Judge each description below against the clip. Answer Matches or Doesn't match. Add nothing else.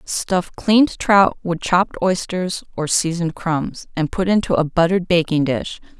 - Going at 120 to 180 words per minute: Matches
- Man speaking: Doesn't match